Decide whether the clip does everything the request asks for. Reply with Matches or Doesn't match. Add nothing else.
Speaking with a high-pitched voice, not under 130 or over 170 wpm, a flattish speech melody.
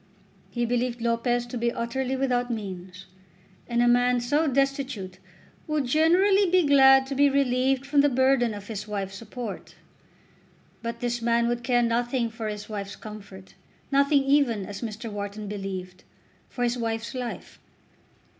Doesn't match